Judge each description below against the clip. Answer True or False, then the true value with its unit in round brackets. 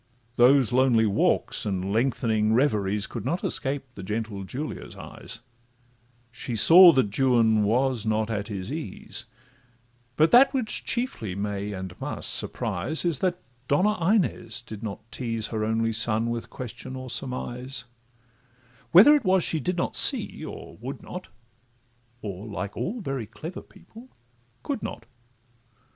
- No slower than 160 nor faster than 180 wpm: False (145 wpm)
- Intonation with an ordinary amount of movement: False (6.3 semitones)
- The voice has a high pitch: False (120 Hz)